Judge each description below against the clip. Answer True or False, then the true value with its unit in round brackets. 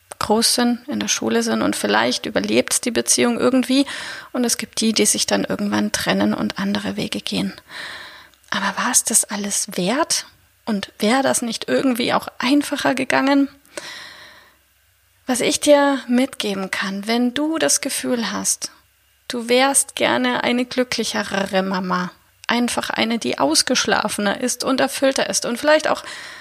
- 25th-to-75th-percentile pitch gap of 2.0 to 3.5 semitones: False (5.5 semitones)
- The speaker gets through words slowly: False (150 wpm)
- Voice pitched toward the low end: False (240 Hz)